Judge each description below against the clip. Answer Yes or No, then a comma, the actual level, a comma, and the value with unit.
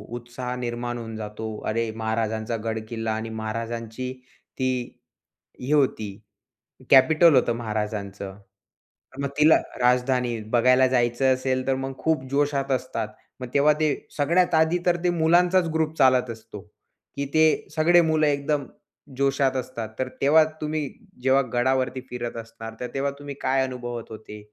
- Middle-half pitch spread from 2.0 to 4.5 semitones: Yes, average, 3.7 semitones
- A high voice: No, low, 130 Hz